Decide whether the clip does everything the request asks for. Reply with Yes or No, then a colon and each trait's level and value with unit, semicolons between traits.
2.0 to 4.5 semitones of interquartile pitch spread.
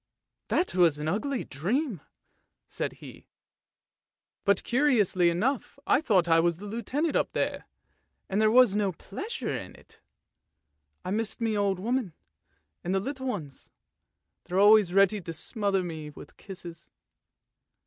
No: average, 5.1 semitones